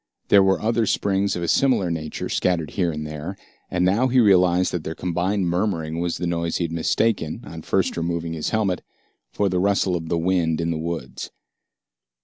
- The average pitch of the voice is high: No, very low, 90 Hz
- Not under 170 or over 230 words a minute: Yes, average, 195 wpm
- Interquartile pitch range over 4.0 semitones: No, average, 2.8 semitones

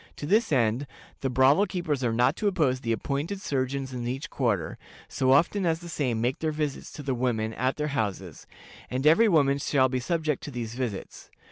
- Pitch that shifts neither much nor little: Yes, average, 3.9 semitones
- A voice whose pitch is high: No, low, 135 Hz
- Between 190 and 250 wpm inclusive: Yes, fast, 205 wpm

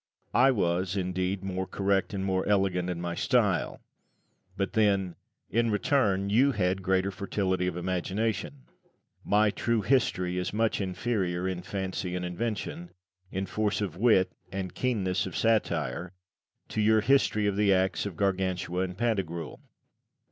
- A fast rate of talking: No, average, 150 wpm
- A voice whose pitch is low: Yes, very low, 95 Hz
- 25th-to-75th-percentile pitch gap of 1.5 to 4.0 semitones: Yes, narrow, 2.6 semitones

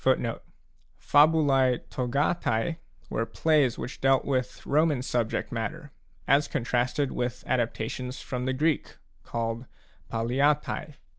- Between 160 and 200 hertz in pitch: No, low, 130 Hz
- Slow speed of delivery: Yes, slow, 105 wpm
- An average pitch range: Yes, average, 3.2 semitones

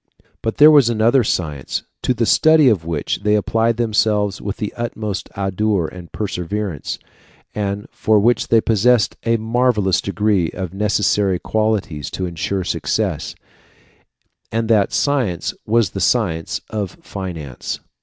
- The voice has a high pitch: No, low, 105 Hz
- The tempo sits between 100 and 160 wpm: Yes, average, 140 wpm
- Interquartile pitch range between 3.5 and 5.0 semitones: No, average, 3.1 semitones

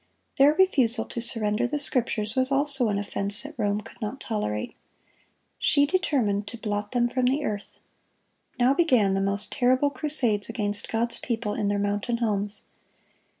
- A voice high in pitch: Yes, high, 230 Hz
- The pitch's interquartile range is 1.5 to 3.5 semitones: No, average, 4.1 semitones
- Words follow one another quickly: No, average, 160 wpm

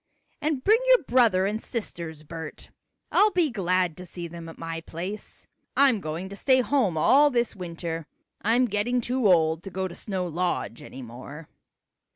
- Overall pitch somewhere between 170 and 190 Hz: Yes, medium, 185 Hz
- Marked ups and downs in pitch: Yes, wide, 6.8 semitones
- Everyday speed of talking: Yes, average, 170 wpm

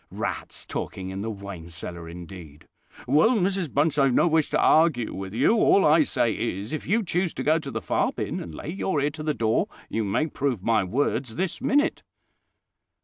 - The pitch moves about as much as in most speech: No, wide, 8.5 semitones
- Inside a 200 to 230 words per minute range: Yes, fast, 205 wpm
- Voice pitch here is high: No, low, 135 Hz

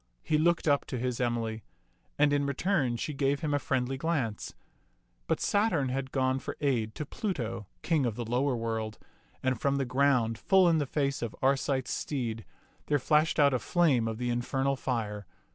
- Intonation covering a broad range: No, average, 3.5 semitones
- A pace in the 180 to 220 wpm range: Yes, average, 190 wpm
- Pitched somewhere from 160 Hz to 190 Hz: No, low, 135 Hz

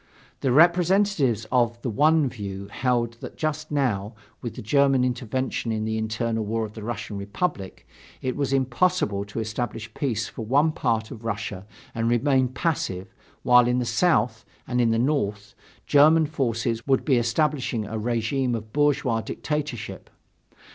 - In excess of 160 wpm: No, average, 155 wpm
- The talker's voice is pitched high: No, low, 120 Hz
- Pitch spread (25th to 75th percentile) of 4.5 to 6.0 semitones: No, average, 4.0 semitones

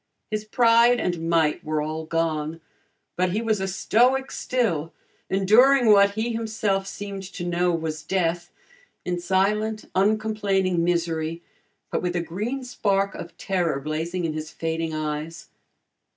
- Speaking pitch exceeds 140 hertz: Yes, medium, 185 Hz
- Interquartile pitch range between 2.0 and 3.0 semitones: No, average, 4.5 semitones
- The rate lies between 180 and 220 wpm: No, average, 140 wpm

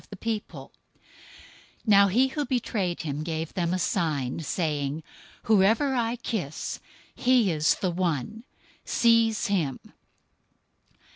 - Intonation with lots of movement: Yes, wide, 6.2 semitones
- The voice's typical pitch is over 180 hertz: Yes, high, 190 Hz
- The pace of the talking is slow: Yes, slow, 110 wpm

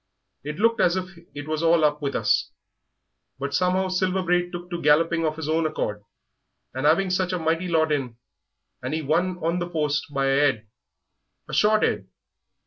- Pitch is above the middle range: No, medium, 165 Hz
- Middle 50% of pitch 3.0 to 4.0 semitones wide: Yes, average, 3.4 semitones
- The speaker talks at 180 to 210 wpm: Yes, average, 190 wpm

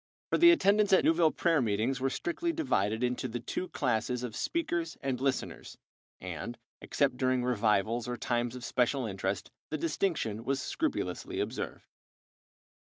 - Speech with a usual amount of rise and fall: No, wide, 6.0 semitones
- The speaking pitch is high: No, low, 125 Hz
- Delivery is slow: No, average, 150 wpm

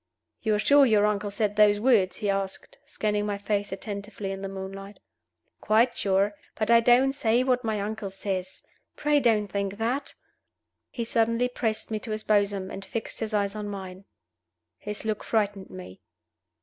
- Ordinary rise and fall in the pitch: No, narrow, 2.2 semitones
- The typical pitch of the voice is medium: No, high, 210 Hz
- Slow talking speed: No, average, 175 wpm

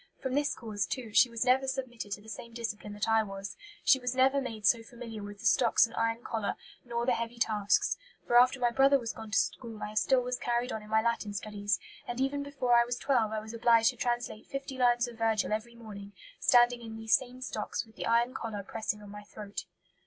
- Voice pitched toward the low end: No, high, 230 Hz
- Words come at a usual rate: No, fast, 235 wpm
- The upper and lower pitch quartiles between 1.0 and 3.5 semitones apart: Yes, narrow, 2.4 semitones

